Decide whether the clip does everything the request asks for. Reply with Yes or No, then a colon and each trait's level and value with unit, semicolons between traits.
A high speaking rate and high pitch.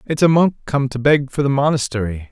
No: fast, 235 wpm; low, 135 Hz